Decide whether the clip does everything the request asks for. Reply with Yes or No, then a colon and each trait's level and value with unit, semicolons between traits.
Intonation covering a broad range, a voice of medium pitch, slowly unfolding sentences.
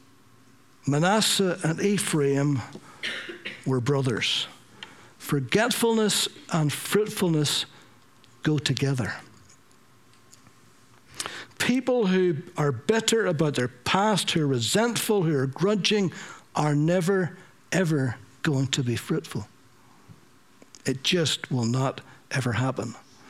Yes: wide, 6.1 semitones; medium, 145 Hz; slow, 95 wpm